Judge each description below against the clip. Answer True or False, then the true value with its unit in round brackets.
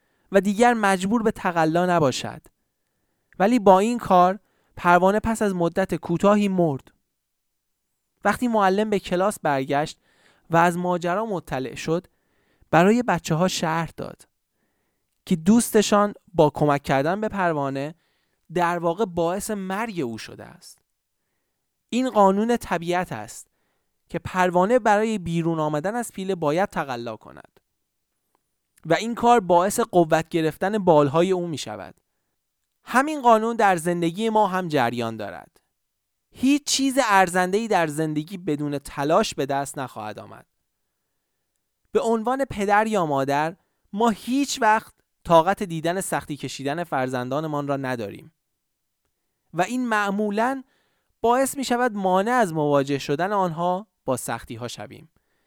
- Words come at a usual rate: True (130 wpm)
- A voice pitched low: False (180 Hz)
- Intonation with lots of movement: True (6.0 semitones)